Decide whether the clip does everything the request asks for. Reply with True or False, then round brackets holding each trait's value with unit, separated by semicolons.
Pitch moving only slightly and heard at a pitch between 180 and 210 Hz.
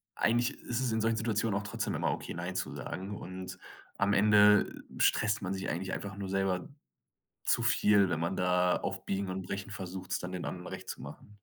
False (2.1 semitones; 95 Hz)